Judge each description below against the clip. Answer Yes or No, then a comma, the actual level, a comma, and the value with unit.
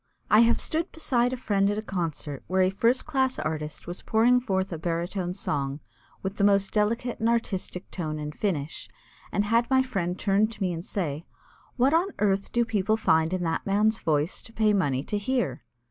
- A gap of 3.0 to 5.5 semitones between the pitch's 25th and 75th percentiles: Yes, average, 5.1 semitones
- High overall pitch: Yes, high, 200 Hz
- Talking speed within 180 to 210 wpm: Yes, average, 200 wpm